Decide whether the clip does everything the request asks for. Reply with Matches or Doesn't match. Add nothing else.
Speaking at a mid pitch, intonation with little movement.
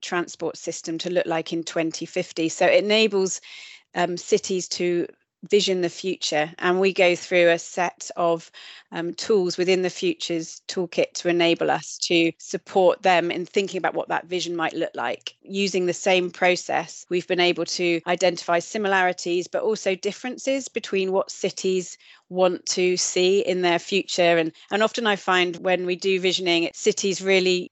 Matches